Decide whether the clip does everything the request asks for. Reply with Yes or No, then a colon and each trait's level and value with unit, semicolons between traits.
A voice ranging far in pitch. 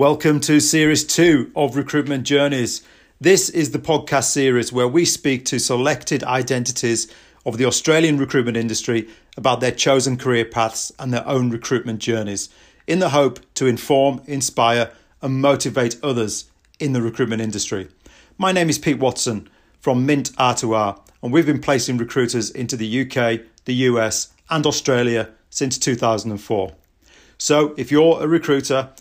No: average, 3.6 semitones